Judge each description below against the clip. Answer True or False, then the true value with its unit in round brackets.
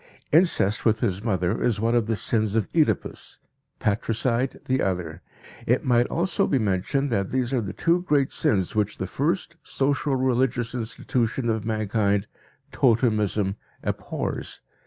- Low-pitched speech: True (115 Hz)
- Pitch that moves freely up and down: False (4.1 semitones)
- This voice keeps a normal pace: True (145 wpm)